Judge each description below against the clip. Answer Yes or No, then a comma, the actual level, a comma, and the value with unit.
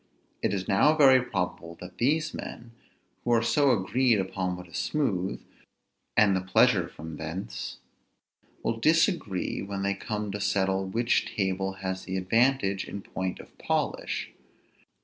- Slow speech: No, average, 150 wpm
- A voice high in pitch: No, low, 100 Hz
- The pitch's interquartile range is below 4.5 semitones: Yes, average, 4.1 semitones